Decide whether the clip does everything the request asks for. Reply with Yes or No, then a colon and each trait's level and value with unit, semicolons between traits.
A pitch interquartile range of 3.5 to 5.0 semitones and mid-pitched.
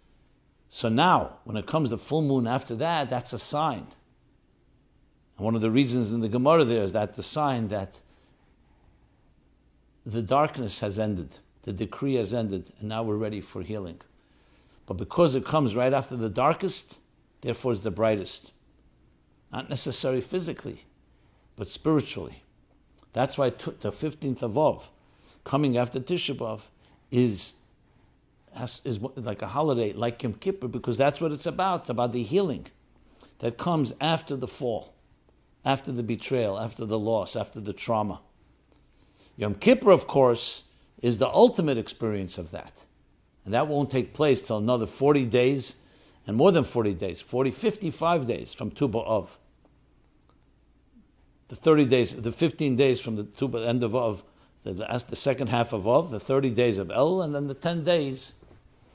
No: average, 4.5 semitones; low, 125 Hz